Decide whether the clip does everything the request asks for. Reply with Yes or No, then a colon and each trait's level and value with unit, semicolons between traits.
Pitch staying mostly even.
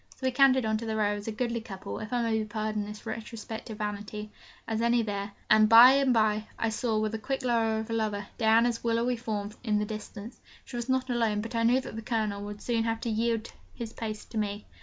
Yes: narrow, 1.7 semitones